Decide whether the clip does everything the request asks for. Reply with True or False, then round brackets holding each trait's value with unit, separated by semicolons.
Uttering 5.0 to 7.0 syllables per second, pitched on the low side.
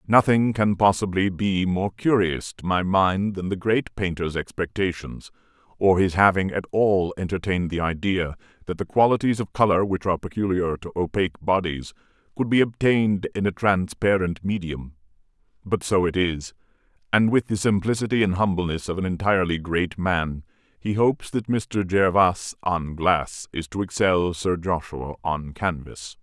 False (4.8 syllables/s; 95 Hz)